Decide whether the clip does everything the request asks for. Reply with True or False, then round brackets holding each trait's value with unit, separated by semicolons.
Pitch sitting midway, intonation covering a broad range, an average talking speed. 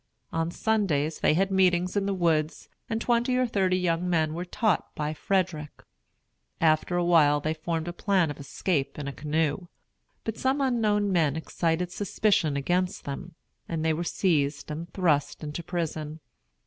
False (170 Hz; 3.6 semitones; 165 wpm)